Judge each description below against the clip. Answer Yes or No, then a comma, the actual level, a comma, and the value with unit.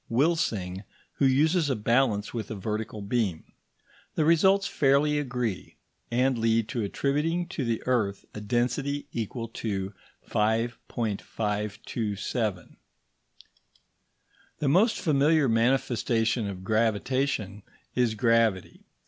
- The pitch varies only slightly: No, average, 4.4 semitones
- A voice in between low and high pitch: No, low, 115 Hz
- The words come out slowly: Yes, slow, 105 wpm